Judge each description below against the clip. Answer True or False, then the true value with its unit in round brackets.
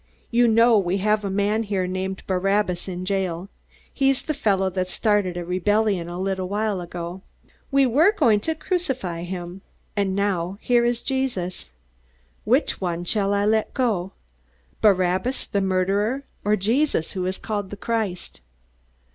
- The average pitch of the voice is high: True (200 Hz)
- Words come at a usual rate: True (150 wpm)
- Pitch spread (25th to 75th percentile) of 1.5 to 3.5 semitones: True (3.2 semitones)